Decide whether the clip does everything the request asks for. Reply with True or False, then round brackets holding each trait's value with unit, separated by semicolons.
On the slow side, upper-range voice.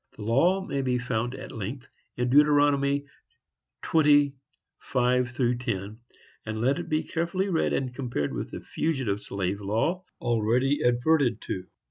False (130 wpm; 125 Hz)